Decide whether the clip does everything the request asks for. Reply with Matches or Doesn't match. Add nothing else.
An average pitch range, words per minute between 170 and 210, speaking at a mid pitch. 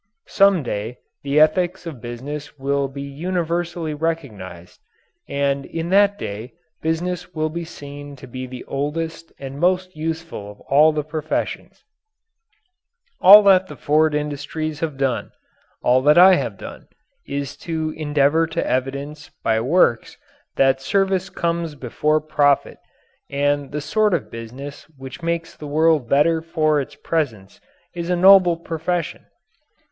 Doesn't match